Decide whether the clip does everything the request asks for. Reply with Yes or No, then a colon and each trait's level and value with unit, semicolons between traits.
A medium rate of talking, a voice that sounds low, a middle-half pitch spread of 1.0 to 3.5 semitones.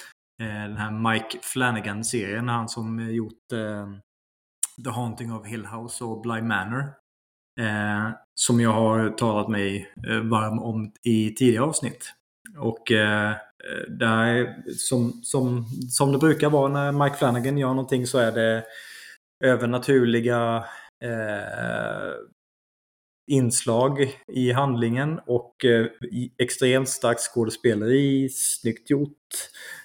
No: slow, 115 wpm; low, 115 Hz; narrow, 2.4 semitones